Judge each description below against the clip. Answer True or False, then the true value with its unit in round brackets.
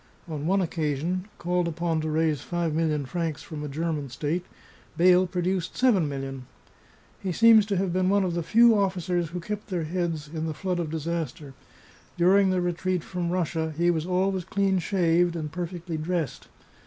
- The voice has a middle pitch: True (175 Hz)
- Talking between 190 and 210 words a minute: False (180 wpm)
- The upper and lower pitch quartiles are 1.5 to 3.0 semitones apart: True (2.6 semitones)